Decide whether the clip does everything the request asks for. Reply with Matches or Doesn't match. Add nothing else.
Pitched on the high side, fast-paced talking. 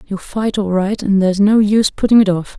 Matches